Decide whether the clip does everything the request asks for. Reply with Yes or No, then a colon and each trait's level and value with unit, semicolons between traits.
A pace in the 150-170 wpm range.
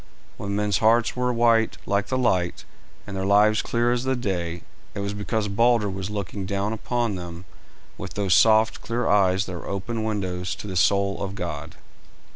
No: average, 185 wpm